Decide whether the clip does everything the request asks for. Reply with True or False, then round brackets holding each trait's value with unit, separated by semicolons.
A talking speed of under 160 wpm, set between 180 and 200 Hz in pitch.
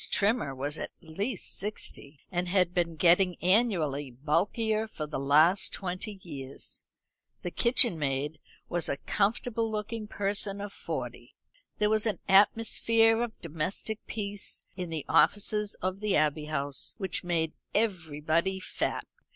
True (135 wpm; 185 Hz)